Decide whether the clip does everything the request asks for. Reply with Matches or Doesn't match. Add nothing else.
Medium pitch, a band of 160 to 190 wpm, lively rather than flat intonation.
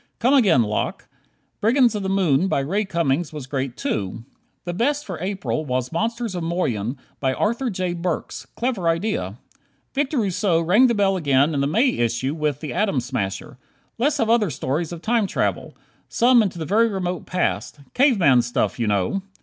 Matches